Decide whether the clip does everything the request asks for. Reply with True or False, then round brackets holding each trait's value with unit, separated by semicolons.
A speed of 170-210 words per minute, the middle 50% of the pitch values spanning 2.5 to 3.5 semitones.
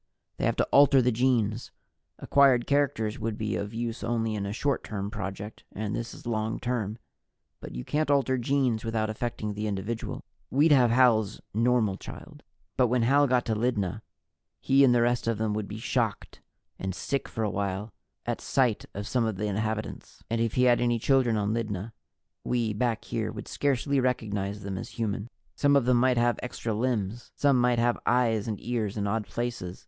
True (195 wpm; 2.8 semitones)